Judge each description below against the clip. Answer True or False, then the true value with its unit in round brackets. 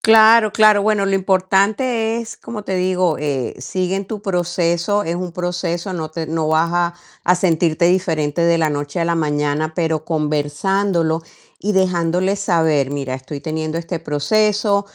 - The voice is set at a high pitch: False (175 Hz)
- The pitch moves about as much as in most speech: True (3.8 semitones)